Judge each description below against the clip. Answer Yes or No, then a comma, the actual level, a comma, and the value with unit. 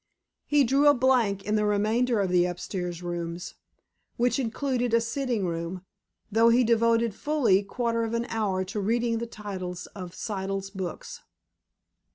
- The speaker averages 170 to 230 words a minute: No, average, 155 wpm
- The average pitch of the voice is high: Yes, high, 215 Hz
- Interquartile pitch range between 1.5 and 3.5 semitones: No, average, 3.9 semitones